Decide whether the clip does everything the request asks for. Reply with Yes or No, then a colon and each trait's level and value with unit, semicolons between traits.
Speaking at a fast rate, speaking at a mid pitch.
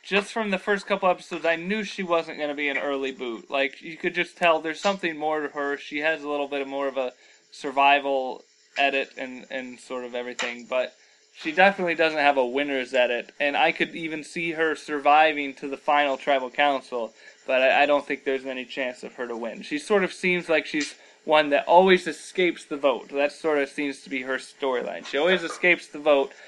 Yes: fast, 220 wpm; medium, 145 Hz